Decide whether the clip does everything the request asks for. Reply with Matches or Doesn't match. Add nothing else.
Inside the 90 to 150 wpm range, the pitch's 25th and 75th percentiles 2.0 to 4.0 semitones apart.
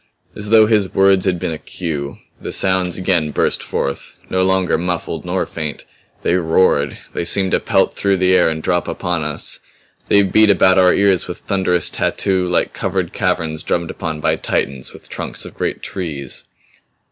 Doesn't match